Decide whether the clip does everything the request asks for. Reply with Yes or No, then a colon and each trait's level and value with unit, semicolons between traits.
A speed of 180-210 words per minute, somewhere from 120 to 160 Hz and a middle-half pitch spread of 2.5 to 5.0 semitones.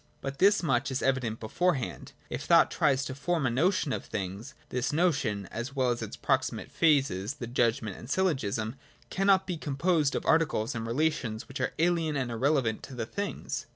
No: average, 185 wpm; low, 135 Hz; wide, 5.4 semitones